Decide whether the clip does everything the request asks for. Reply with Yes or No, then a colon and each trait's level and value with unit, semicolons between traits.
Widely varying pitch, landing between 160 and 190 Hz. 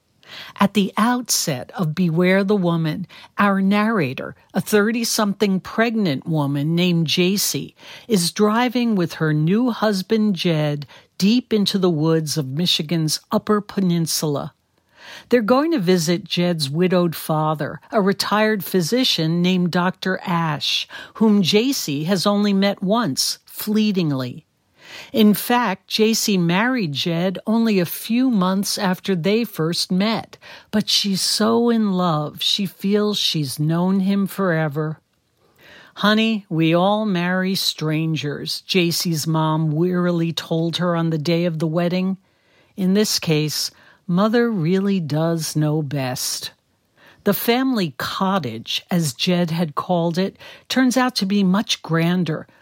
No: average, 4.1 semitones; medium, 185 Hz